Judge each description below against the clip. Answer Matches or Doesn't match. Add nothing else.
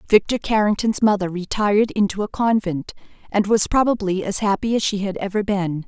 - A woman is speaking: Matches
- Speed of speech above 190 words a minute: Doesn't match